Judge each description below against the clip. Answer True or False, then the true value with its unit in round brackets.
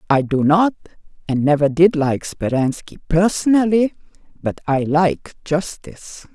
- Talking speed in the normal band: False (125 wpm)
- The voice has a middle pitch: True (165 Hz)